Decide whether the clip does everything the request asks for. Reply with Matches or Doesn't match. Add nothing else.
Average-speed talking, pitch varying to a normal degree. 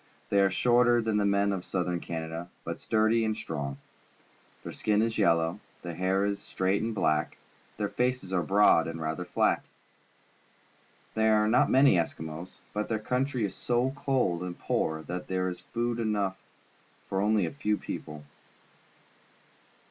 Matches